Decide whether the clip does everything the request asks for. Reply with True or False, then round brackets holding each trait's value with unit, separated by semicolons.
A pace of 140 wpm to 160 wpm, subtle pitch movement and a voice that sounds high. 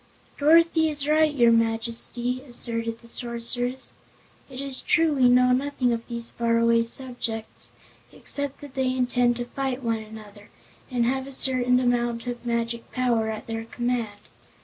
True (150 wpm; 2.1 semitones; 245 Hz)